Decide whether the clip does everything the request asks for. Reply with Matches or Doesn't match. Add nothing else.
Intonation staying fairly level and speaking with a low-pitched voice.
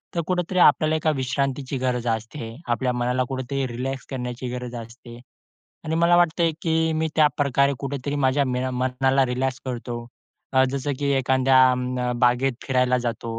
Matches